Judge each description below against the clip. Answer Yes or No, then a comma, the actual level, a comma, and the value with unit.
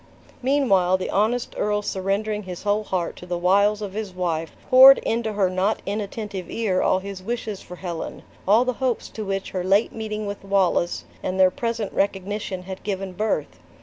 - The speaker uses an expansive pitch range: No, narrow, 2.5 semitones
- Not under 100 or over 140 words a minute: No, average, 180 wpm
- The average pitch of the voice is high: Yes, high, 200 Hz